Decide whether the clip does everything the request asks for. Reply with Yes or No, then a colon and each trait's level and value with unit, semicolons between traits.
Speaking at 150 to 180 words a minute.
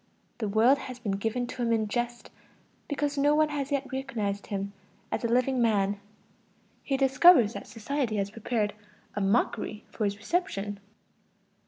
Yes: average, 160 wpm